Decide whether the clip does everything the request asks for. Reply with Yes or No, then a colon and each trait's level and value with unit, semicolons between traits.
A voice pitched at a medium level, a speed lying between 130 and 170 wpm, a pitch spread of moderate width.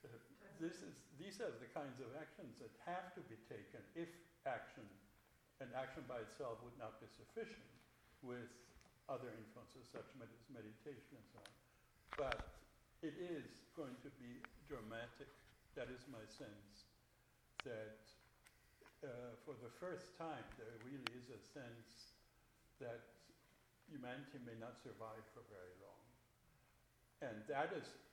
No: low, 125 Hz; average, 140 wpm; average, 4.0 semitones